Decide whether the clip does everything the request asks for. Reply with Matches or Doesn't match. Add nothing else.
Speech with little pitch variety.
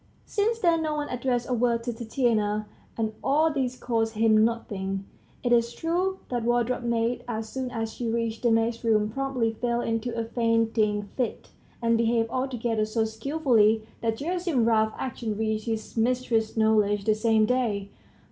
Matches